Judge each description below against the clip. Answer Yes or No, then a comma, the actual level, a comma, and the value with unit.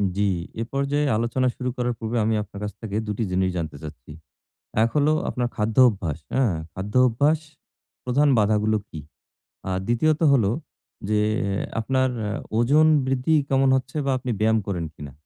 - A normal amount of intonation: Yes, average, 4.5 semitones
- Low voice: Yes, low, 115 Hz